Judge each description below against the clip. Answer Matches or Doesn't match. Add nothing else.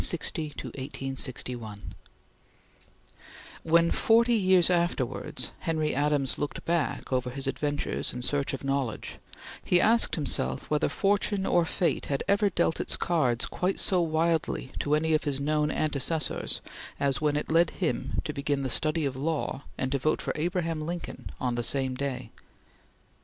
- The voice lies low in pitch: Doesn't match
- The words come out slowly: Doesn't match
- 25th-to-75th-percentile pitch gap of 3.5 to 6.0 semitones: Matches